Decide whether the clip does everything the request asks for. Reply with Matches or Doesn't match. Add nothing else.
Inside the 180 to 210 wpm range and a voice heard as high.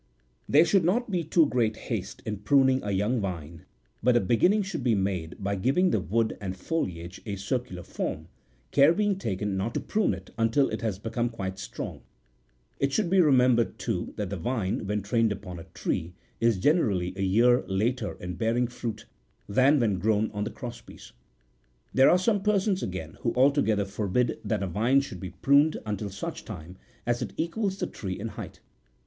Doesn't match